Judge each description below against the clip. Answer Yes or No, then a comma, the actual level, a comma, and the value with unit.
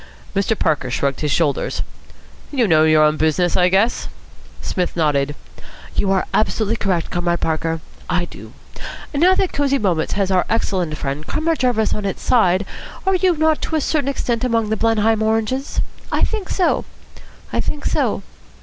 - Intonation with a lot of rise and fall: Yes, wide, 7.4 semitones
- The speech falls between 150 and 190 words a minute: Yes, average, 170 wpm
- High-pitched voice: Yes, high, 200 Hz